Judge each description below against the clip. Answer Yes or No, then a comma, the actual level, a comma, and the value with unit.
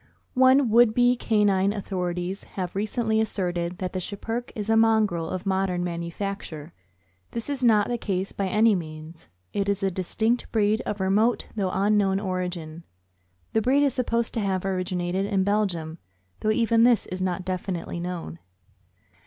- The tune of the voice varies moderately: Yes, average, 3.4 semitones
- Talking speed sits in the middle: Yes, average, 160 wpm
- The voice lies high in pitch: Yes, high, 195 Hz